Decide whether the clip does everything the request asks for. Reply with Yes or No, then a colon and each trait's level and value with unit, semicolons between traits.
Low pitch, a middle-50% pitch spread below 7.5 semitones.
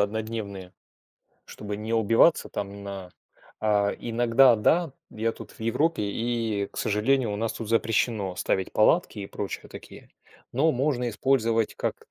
Yes: low, 110 Hz; average, 2.8 semitones